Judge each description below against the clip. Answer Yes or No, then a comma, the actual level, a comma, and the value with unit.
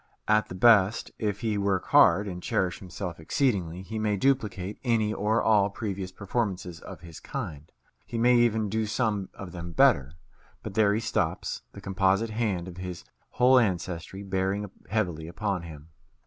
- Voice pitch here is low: Yes, low, 100 Hz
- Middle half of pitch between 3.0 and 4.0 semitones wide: Yes, average, 3.3 semitones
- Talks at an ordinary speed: Yes, average, 165 wpm